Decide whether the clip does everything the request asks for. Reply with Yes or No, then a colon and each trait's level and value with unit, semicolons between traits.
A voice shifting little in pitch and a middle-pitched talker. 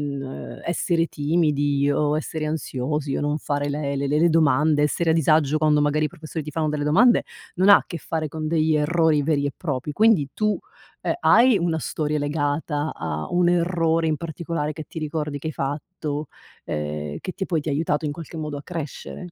Yes: narrow, 2.1 semitones; medium, 155 Hz